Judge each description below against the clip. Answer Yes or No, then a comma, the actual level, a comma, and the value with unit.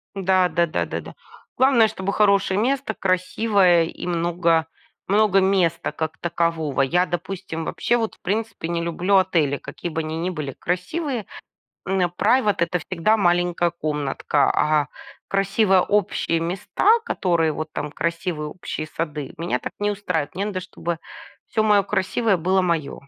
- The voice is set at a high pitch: No, medium, 180 Hz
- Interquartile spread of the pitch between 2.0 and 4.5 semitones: Yes, average, 3.3 semitones